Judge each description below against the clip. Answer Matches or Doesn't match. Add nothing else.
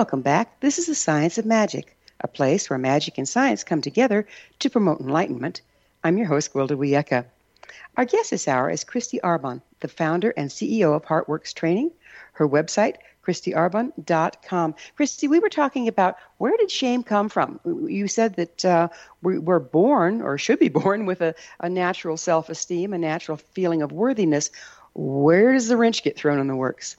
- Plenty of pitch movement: Matches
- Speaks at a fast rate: Doesn't match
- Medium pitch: Matches